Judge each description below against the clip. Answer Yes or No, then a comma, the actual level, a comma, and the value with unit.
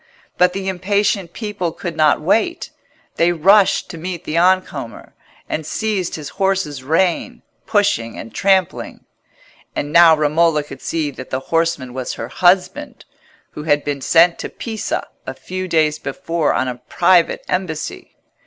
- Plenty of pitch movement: No, average, 3.9 semitones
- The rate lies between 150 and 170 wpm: Yes, average, 155 wpm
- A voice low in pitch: No, medium, 170 Hz